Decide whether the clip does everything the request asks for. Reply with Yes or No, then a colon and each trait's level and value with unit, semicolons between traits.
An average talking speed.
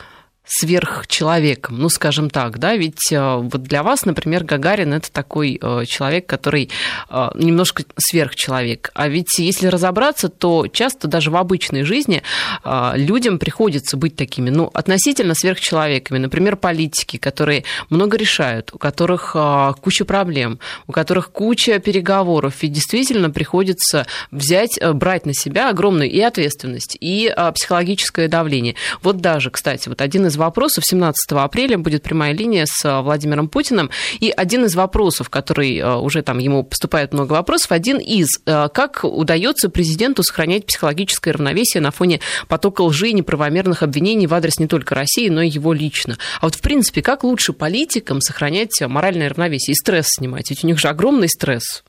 Yes: average, 150 wpm